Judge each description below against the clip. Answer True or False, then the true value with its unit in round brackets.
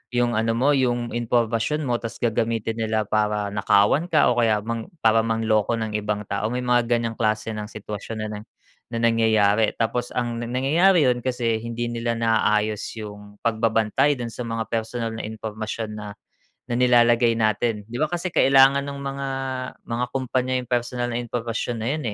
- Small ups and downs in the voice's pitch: True (1.9 semitones)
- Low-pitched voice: True (115 Hz)